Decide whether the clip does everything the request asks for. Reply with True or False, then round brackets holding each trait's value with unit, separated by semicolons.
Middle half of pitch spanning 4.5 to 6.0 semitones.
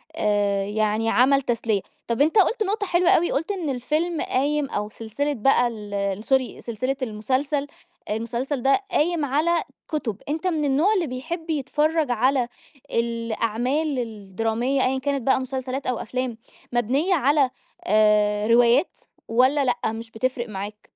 True (4.8 semitones)